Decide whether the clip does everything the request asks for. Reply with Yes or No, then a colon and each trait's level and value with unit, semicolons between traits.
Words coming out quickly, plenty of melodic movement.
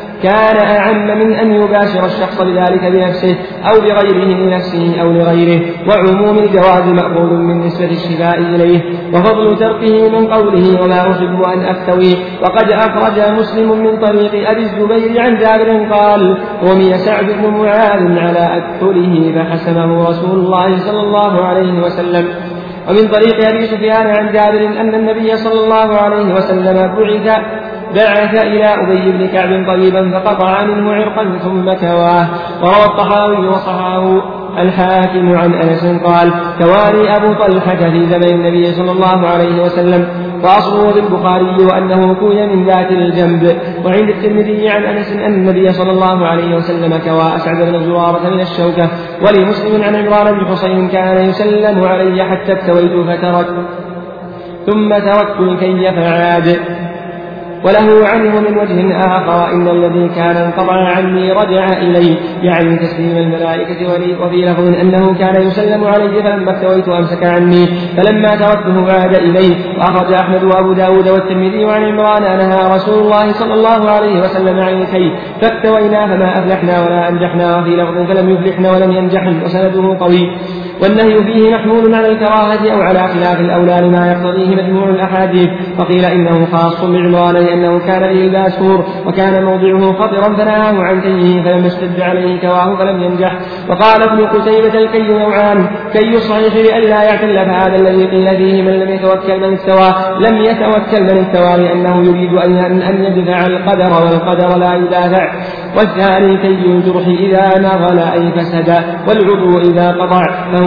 No: fast, 140 wpm; average, 2.7 semitones